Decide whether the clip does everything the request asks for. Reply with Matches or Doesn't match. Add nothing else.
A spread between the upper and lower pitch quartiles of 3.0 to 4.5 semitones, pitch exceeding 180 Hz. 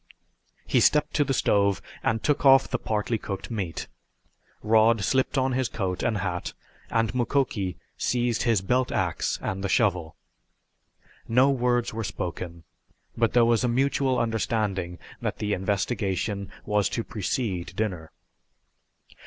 Doesn't match